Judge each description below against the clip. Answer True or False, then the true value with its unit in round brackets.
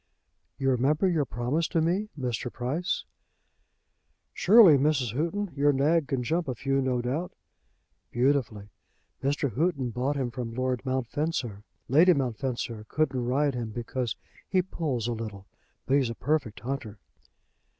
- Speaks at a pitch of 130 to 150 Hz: True (135 Hz)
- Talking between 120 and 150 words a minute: True (140 wpm)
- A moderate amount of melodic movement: True (4.2 semitones)